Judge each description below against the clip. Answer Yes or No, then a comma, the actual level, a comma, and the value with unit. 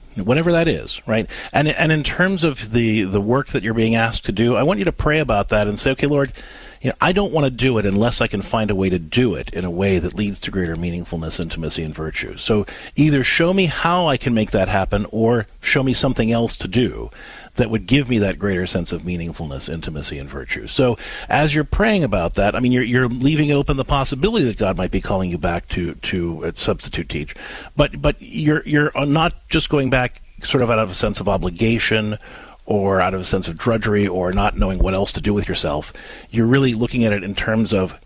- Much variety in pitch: Yes, wide, 6.4 semitones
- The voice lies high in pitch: No, low, 110 Hz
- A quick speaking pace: Yes, fast, 245 wpm